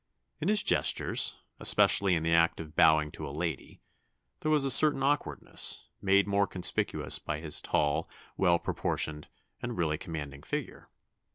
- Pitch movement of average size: Yes, average, 4.7 semitones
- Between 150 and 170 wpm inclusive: Yes, average, 155 wpm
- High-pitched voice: No, very low, 85 Hz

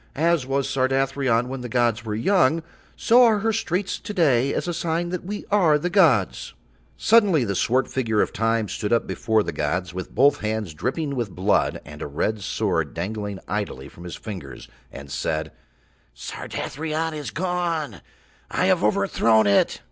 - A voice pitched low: Yes, low, 125 Hz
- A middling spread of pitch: No, wide, 7.9 semitones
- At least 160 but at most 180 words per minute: Yes, average, 170 wpm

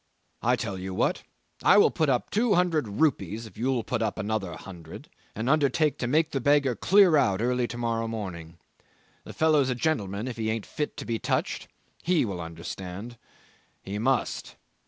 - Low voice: Yes, low, 120 Hz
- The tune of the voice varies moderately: No, wide, 6.3 semitones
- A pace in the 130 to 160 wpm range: No, average, 180 wpm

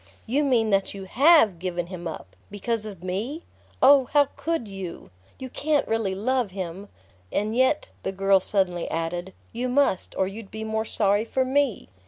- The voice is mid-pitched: No, high, 210 Hz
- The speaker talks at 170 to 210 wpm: Yes, average, 175 wpm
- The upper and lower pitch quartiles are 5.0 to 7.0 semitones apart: Yes, average, 5.3 semitones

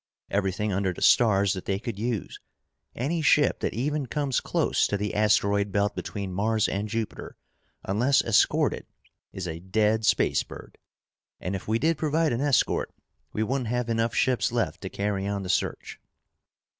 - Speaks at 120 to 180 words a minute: Yes, average, 170 wpm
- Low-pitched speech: Yes, low, 110 Hz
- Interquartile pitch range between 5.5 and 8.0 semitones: No, average, 3.5 semitones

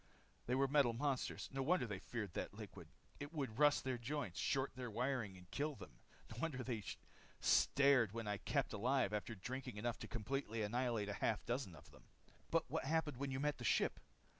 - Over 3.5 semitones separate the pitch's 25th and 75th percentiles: Yes, average, 4.2 semitones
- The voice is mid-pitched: No, low, 125 Hz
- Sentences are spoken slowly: No, average, 200 wpm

